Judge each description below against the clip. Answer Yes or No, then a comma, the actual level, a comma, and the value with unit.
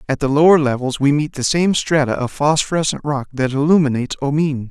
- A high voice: No, medium, 145 Hz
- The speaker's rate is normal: Yes, average, 190 wpm